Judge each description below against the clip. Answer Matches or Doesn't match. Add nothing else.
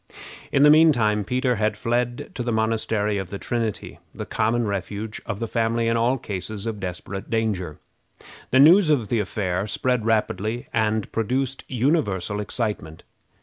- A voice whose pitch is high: Doesn't match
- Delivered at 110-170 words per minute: Matches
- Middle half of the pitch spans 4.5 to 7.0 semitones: Doesn't match